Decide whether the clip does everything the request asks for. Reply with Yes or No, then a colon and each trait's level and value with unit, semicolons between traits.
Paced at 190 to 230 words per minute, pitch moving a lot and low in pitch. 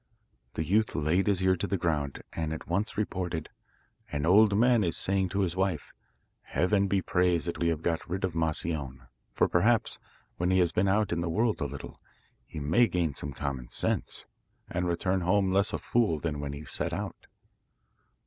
No: average, 195 wpm; average, 3.6 semitones; very low, 90 Hz